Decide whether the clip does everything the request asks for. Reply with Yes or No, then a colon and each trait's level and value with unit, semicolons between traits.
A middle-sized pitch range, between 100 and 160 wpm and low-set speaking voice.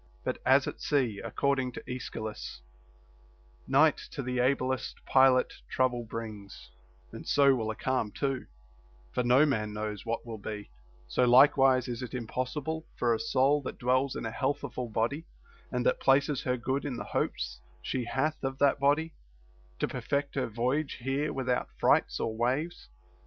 No: average, 3.0 semitones; average, 170 wpm; low, 130 Hz